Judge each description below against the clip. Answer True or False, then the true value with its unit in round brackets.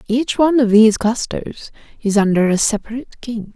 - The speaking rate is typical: True (170 wpm)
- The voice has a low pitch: False (230 Hz)